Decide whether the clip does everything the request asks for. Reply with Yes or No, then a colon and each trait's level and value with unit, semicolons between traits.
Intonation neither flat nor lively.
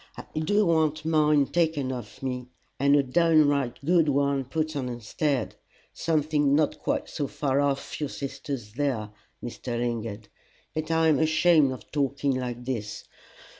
Yes: average, 3.5 semitones